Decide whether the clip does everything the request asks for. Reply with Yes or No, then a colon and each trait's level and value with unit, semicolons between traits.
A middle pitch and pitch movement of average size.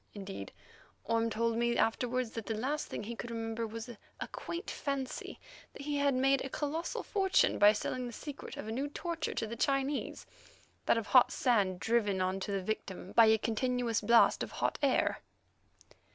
No: high, 235 Hz; average, 3.7 semitones